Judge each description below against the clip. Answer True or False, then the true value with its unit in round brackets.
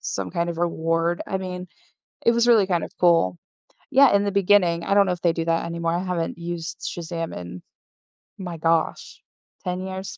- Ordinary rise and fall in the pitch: False (2.2 semitones)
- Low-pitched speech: False (175 Hz)